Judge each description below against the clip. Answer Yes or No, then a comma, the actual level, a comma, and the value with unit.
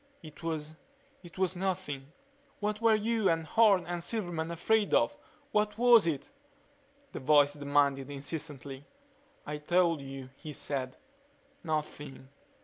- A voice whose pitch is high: No, medium, 160 Hz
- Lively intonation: No, average, 4.9 semitones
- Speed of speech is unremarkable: No, slow, 130 wpm